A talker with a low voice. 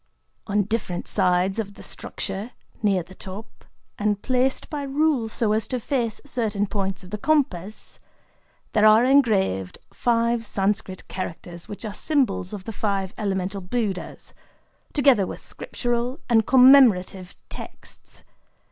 No: high, 210 Hz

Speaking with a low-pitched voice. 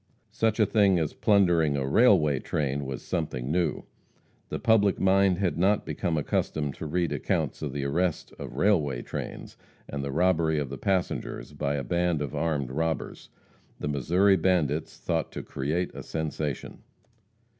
Yes: very low, 80 Hz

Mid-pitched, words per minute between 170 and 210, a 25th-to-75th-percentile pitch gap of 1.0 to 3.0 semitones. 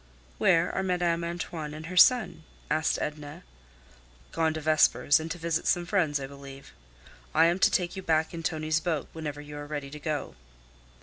Yes: medium, 160 Hz; average, 185 wpm; narrow, 2.4 semitones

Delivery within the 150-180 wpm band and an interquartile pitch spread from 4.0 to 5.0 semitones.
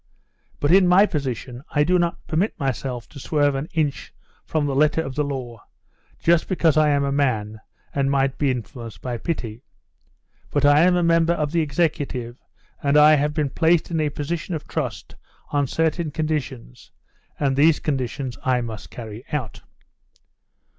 No: average, 170 wpm; average, 3.6 semitones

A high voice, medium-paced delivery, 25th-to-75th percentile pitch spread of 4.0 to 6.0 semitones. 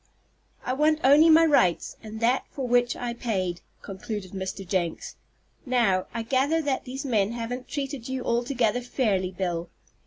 Yes: high, 240 Hz; average, 155 wpm; average, 5.2 semitones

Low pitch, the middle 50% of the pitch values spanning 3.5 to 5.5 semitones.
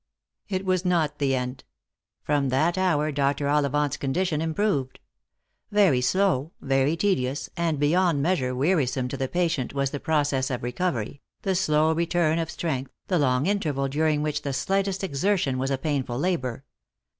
No: medium, 150 Hz; average, 4.5 semitones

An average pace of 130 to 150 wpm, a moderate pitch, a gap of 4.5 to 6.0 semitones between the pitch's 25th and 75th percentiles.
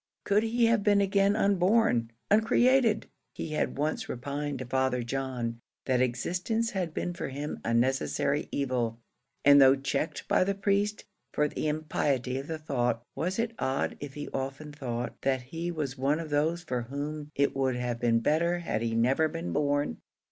No: average, 175 wpm; medium, 145 Hz; average, 5.3 semitones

